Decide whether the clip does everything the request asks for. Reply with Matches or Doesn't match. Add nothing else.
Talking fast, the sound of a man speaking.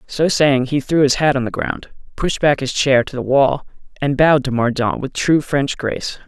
Matches